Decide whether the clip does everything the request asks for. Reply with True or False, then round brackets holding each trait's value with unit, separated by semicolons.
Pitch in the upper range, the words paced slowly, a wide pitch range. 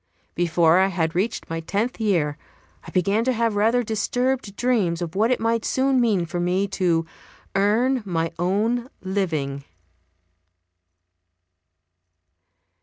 False (200 Hz; 125 wpm; 5.0 semitones)